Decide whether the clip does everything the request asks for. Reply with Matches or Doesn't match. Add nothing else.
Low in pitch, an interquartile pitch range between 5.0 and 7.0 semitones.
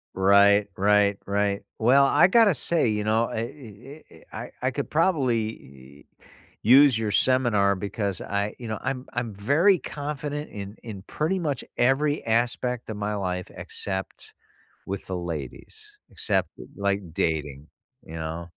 Matches